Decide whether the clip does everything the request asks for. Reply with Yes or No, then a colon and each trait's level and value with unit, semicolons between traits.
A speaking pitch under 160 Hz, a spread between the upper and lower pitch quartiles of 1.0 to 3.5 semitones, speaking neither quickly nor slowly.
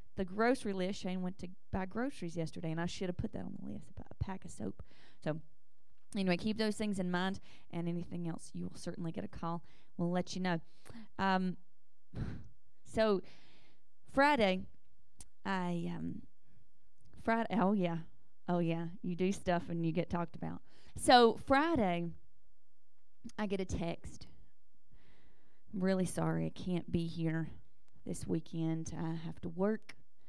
No: medium, 180 Hz; average, 2.7 semitones; average, 160 wpm